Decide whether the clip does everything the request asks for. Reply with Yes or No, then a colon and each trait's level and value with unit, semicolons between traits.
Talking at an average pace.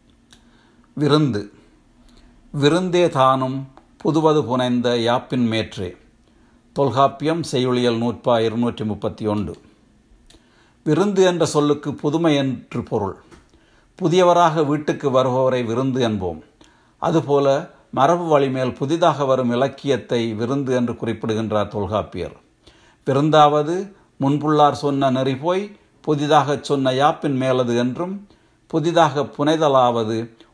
Yes: average, 90 wpm